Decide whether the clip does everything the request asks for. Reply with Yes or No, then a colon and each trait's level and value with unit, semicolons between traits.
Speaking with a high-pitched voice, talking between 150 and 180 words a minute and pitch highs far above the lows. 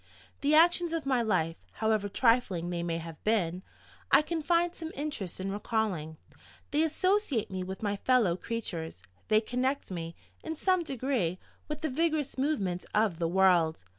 Yes: high, 220 Hz; average, 165 wpm; wide, 8.9 semitones